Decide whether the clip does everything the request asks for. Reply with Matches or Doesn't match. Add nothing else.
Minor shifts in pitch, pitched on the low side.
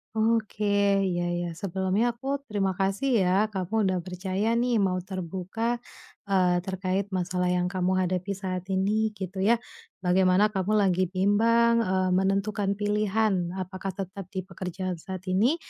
Doesn't match